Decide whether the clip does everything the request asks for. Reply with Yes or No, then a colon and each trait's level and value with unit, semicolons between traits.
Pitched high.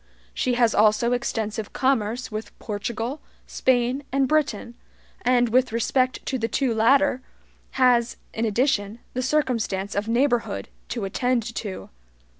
Yes: high, 240 Hz